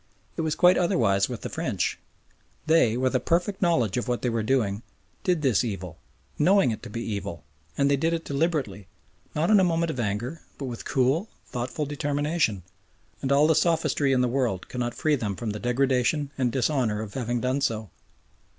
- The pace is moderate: Yes, average, 195 wpm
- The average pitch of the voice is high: No, low, 130 Hz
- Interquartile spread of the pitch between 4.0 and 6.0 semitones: Yes, average, 5.2 semitones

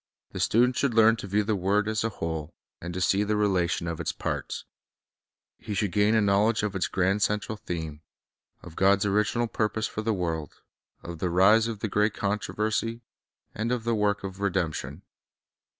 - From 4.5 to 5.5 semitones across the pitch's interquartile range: No, average, 2.8 semitones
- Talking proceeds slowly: No, average, 185 wpm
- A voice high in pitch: No, low, 105 Hz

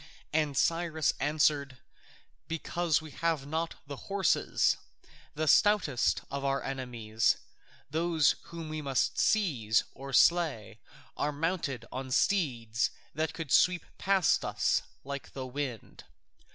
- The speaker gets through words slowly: Yes, slow, 120 wpm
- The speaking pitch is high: No, medium, 145 Hz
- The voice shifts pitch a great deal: No, average, 3.8 semitones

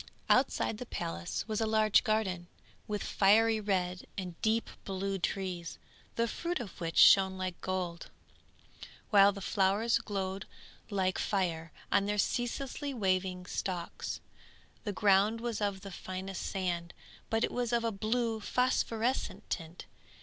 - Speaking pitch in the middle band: No, high, 200 Hz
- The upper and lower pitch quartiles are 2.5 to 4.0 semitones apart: Yes, average, 3.0 semitones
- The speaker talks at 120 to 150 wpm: Yes, average, 140 wpm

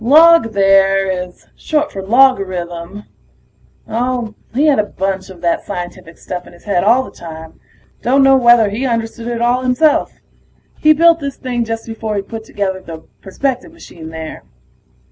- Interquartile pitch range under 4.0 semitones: No, average, 5.2 semitones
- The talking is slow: No, average, 165 wpm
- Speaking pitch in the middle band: No, high, 220 Hz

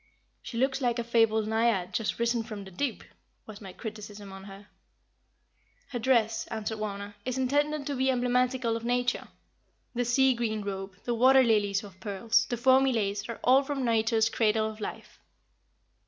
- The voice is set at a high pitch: Yes, high, 230 Hz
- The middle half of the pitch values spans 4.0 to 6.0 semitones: No, average, 3.0 semitones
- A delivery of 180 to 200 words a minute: No, average, 170 wpm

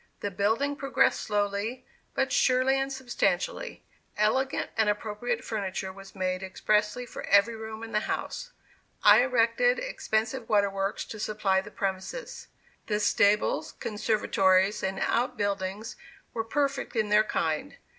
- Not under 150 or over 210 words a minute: No, slow, 135 wpm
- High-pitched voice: Yes, high, 215 Hz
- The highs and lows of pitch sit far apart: No, average, 3.8 semitones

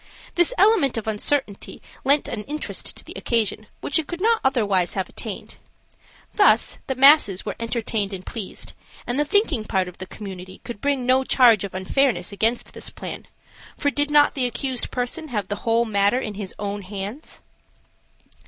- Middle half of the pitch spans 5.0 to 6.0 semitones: Yes, wide, 5.6 semitones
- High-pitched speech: Yes, high, 235 Hz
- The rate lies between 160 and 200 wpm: Yes, average, 175 wpm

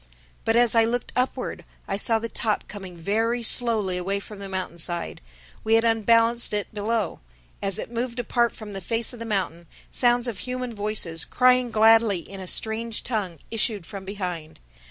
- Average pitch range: Yes, average, 3.0 semitones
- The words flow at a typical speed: Yes, average, 175 wpm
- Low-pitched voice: No, high, 220 Hz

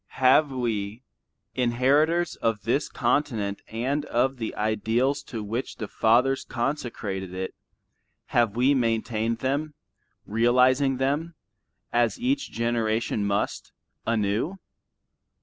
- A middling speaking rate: No, slow, 105 wpm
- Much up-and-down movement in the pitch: No, average, 3.4 semitones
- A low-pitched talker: Yes, low, 120 Hz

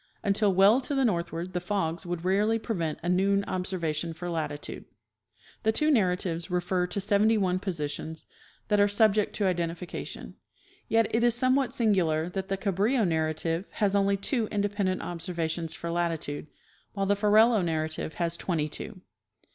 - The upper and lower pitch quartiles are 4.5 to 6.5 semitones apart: No, average, 3.6 semitones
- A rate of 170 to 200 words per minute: No, average, 160 wpm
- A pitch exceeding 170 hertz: Yes, medium, 185 Hz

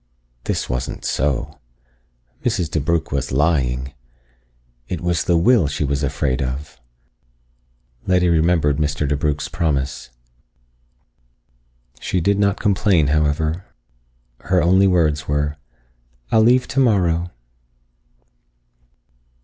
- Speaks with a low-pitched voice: Yes, very low, 80 Hz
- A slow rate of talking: Yes, slow, 100 wpm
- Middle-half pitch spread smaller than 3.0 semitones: No, average, 3.7 semitones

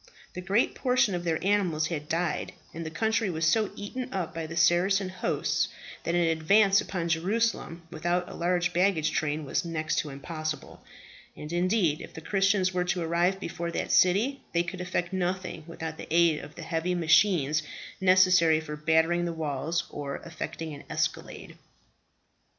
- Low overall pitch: No, medium, 170 Hz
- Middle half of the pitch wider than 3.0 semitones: No, average, 2.7 semitones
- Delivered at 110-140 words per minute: No, average, 170 wpm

